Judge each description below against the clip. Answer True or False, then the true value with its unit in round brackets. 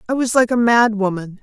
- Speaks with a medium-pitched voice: False (225 Hz)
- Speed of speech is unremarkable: False (210 wpm)